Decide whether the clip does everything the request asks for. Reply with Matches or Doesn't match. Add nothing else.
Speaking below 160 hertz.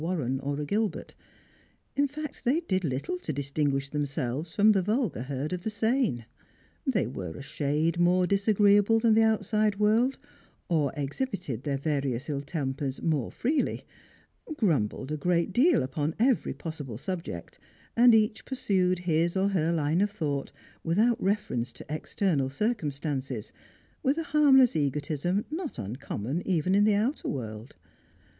Doesn't match